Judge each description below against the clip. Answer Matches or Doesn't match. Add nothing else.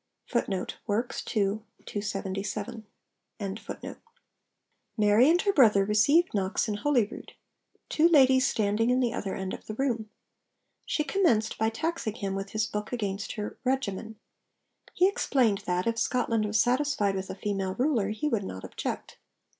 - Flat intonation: Doesn't match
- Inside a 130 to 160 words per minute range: Matches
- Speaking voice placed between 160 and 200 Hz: Doesn't match